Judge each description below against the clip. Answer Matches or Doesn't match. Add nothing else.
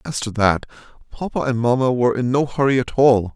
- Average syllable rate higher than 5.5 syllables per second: Matches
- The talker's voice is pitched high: Doesn't match